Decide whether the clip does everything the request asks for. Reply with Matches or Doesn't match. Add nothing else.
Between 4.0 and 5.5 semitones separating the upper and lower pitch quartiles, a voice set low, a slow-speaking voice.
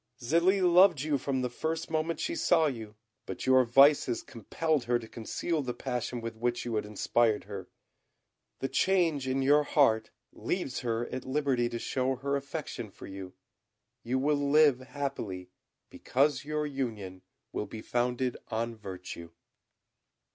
Doesn't match